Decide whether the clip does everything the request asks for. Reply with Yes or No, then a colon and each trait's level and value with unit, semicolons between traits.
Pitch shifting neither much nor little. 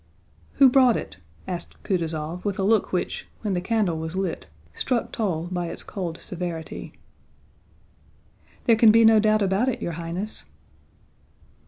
Yes: average, 4.4 semitones